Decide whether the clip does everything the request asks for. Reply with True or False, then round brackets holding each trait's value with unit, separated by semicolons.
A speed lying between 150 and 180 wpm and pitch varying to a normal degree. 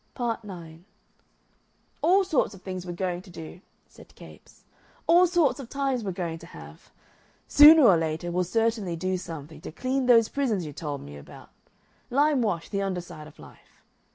False (170 wpm; 7.1 semitones)